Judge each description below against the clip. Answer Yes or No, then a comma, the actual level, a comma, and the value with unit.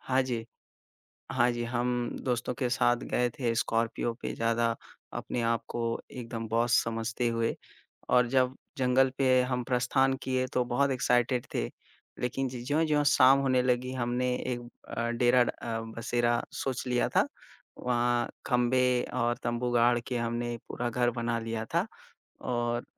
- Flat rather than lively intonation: Yes, narrow, 1.3 semitones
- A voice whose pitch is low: Yes, low, 120 Hz